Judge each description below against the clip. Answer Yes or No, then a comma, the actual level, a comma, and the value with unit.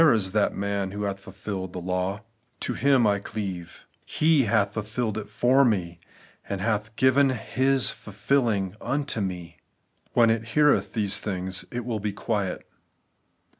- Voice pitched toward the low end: Yes, low, 105 Hz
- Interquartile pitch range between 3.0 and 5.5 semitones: Yes, average, 3.8 semitones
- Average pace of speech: Yes, average, 155 wpm